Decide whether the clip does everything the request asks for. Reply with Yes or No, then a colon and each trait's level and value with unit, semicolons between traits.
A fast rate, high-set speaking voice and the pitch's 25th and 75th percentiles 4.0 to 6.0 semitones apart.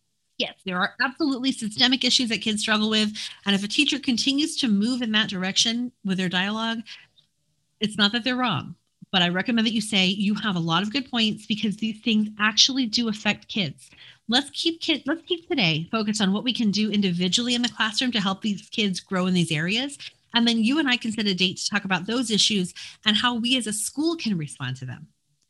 Yes: fast, 225 wpm; high, 215 Hz; average, 4.3 semitones